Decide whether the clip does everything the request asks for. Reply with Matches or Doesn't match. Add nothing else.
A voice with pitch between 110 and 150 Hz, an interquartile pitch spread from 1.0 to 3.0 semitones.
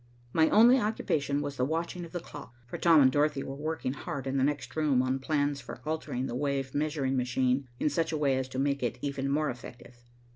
Matches